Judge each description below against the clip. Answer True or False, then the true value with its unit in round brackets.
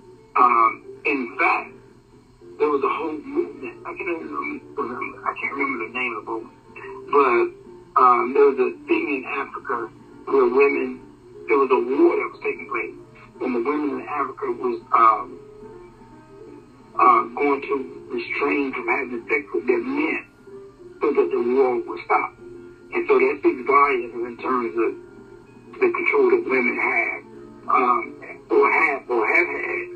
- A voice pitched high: True (370 Hz)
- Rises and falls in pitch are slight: True (1.5 semitones)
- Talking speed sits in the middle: True (160 wpm)